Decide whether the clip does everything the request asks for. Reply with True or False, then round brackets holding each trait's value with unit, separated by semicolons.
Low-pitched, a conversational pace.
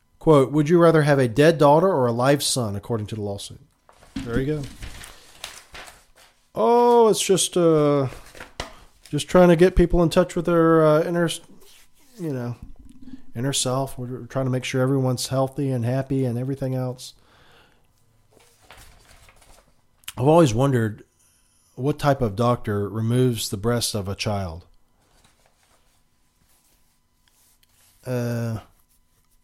False (125 Hz; 130 wpm)